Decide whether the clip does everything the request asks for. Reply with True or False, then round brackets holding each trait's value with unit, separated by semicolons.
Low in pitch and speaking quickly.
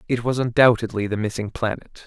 False (115 Hz; 175 wpm)